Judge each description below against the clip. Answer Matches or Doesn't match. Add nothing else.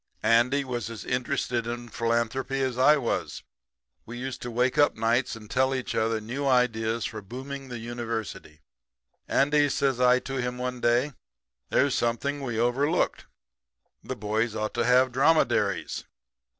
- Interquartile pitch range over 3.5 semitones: Doesn't match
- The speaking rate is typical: Matches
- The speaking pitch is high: Doesn't match